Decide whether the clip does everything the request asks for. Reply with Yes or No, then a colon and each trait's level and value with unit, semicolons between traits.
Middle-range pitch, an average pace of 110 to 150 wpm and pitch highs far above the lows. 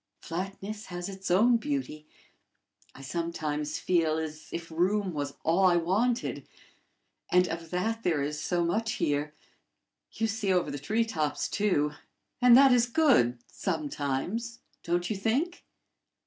Yes: medium, 180 Hz; average, 140 wpm; wide, 6.1 semitones